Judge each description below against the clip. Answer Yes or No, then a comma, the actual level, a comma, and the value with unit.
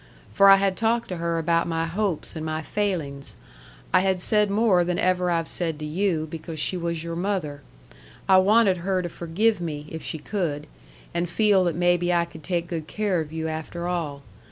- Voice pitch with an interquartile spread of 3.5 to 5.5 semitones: No, average, 2.9 semitones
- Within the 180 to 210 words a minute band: Yes, fast, 205 wpm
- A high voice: No, medium, 175 Hz